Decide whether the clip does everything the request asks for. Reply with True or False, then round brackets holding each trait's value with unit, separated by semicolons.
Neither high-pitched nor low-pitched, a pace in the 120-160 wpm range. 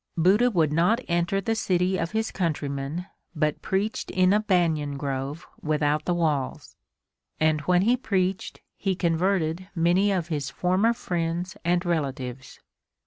True (175 Hz; 140 wpm)